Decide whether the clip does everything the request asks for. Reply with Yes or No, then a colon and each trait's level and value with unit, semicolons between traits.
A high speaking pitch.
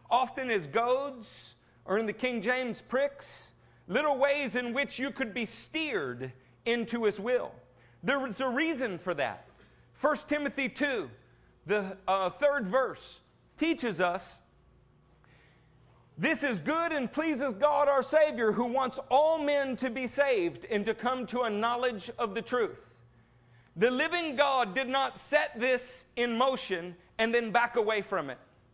Yes: very high, 250 Hz